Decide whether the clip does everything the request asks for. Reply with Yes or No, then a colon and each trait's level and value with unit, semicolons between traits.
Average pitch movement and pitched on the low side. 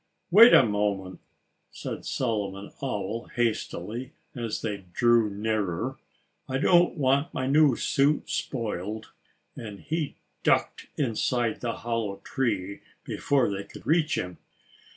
Yes: average, 4.6 semitones; low, 115 Hz